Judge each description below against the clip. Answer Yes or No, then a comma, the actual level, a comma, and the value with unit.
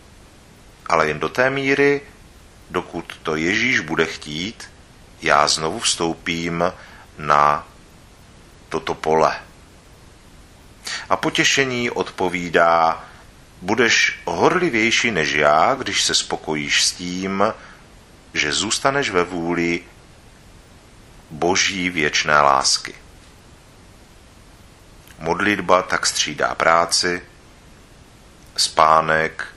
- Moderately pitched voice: No, very low, 85 Hz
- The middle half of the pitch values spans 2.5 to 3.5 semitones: Yes, average, 2.8 semitones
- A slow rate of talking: Yes, slow, 80 wpm